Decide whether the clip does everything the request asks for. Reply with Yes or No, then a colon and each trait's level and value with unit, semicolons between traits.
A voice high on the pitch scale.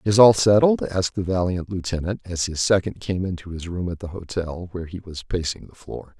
No: very low, 90 Hz